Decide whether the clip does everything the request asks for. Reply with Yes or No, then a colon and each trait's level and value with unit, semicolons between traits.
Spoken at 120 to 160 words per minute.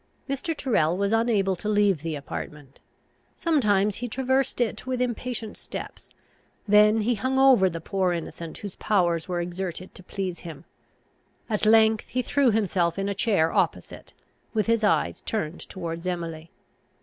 Yes: average, 155 wpm